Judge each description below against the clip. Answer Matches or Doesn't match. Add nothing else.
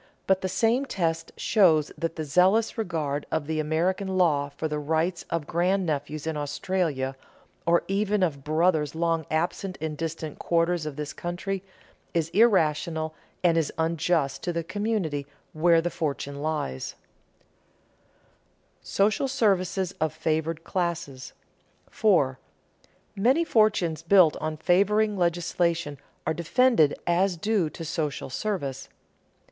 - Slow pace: Matches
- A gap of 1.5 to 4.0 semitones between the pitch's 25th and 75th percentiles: Matches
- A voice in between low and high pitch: Matches